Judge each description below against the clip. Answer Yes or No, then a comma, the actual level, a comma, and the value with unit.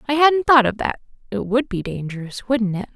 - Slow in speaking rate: No, fast, 205 wpm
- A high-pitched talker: Yes, high, 230 Hz